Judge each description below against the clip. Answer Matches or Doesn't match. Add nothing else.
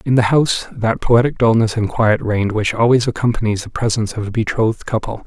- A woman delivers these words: Doesn't match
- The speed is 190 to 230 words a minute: Matches